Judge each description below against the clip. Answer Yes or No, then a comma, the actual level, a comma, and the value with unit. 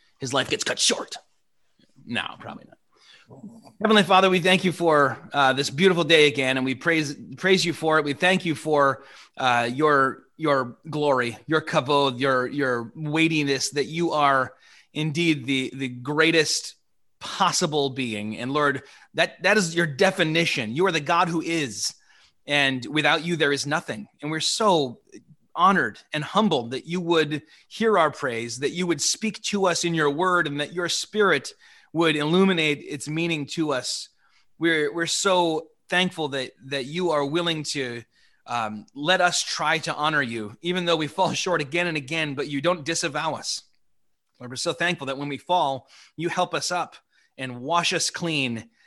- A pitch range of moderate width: Yes, average, 3.7 semitones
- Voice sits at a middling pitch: Yes, medium, 155 Hz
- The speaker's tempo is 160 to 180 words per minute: Yes, average, 175 wpm